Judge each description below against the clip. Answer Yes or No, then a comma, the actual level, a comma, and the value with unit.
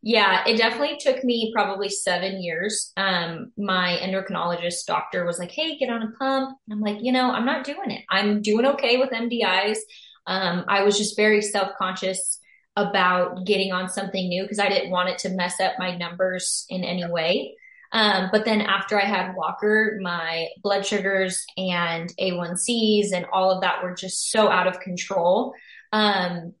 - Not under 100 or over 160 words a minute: No, average, 180 wpm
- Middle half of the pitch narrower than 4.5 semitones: Yes, average, 3.1 semitones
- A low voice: No, high, 195 Hz